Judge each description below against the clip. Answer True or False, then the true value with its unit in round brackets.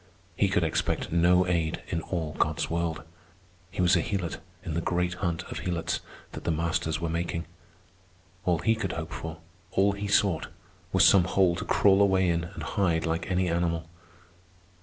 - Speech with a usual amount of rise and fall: False (2.1 semitones)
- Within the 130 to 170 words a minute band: False (180 wpm)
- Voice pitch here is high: False (85 Hz)